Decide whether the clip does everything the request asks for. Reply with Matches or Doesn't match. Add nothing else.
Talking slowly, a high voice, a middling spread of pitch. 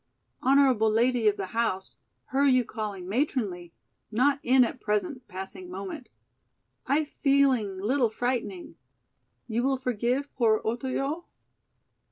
Matches